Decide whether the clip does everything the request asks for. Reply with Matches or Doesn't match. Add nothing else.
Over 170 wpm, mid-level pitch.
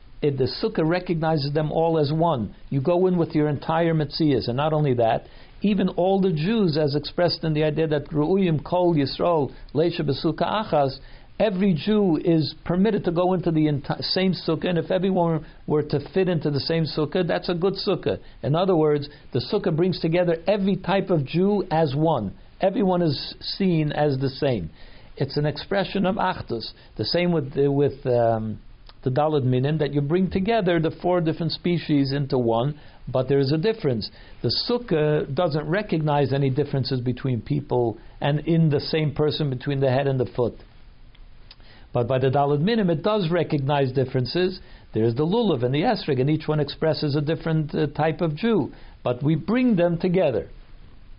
Matches